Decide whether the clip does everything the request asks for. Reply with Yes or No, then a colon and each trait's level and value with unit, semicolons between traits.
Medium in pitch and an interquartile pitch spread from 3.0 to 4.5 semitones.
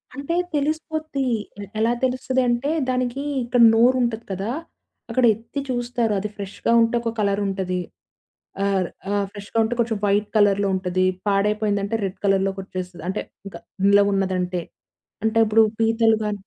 No: high, 215 Hz; average, 3.4 semitones